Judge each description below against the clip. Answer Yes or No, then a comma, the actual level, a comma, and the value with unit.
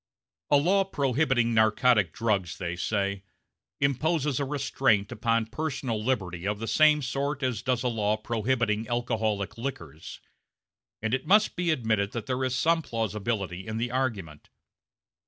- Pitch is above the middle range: No, low, 115 Hz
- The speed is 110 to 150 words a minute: Yes, average, 145 wpm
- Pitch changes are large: No, average, 4.3 semitones